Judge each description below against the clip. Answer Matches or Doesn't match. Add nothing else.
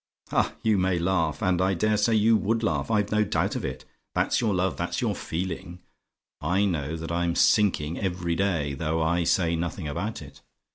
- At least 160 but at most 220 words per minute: Matches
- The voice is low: Matches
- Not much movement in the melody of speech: Doesn't match